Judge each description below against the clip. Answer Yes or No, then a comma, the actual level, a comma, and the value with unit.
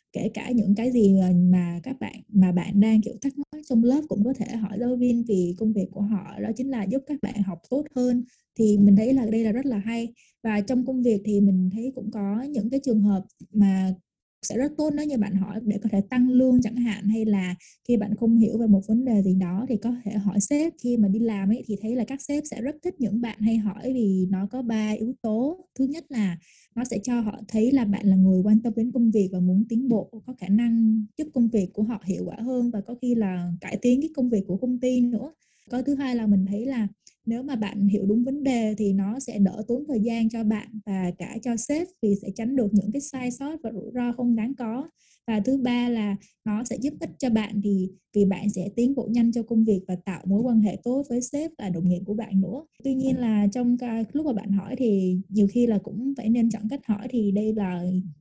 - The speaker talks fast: Yes, fast, 260 wpm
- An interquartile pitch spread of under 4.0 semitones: Yes, average, 3.4 semitones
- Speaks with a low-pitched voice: No, high, 225 Hz